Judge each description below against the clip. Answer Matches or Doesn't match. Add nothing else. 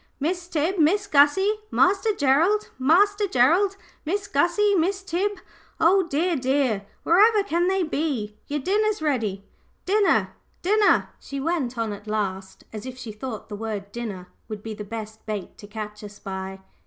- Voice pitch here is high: Matches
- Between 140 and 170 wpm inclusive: Matches